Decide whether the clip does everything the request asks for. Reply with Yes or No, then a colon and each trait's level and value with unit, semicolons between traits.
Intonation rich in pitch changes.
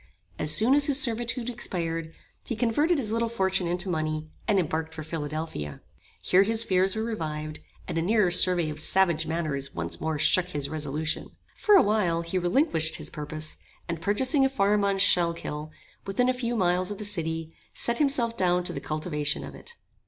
Yes: wide, 6.0 semitones